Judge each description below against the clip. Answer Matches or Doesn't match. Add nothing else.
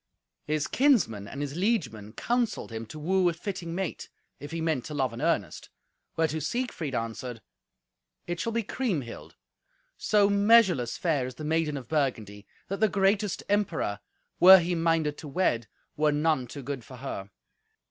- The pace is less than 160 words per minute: Doesn't match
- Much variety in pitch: Matches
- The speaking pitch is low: Doesn't match